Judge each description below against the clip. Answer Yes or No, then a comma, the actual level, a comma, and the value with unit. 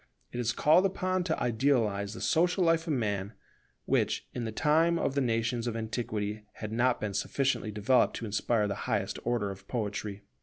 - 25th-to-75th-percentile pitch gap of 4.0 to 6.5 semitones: Yes, average, 5.2 semitones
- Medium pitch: No, low, 115 Hz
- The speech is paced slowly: No, average, 185 wpm